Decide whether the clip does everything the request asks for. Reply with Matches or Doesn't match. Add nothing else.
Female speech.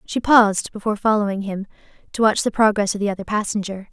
Matches